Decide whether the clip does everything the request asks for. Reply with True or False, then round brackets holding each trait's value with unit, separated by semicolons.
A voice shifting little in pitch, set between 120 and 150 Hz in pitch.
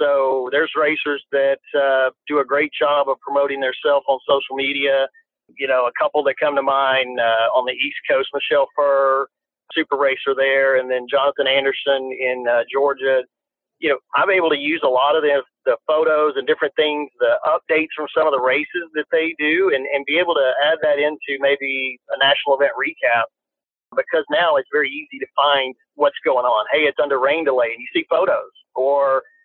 True (2.3 semitones; 140 Hz)